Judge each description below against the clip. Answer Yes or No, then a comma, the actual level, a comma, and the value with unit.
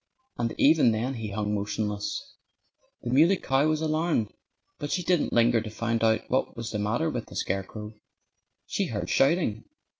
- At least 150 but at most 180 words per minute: Yes, average, 170 wpm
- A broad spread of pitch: Yes, wide, 5.9 semitones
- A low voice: Yes, low, 115 Hz